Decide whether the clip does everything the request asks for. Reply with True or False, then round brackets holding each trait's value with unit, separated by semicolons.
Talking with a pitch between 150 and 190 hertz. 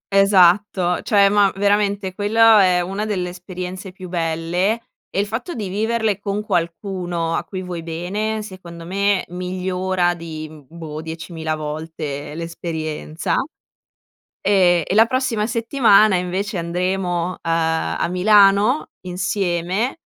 True (185 Hz)